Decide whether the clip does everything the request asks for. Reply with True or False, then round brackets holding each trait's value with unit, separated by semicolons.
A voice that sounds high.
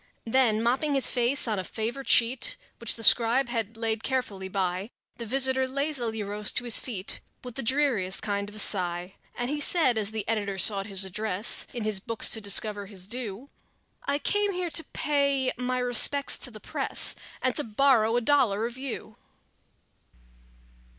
True (230 Hz)